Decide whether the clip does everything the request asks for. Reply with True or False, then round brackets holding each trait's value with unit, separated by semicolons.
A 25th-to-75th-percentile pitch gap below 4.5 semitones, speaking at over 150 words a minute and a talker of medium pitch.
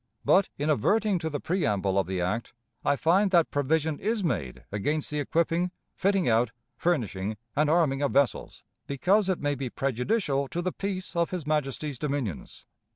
False (5.3 semitones; 170 wpm; 150 Hz)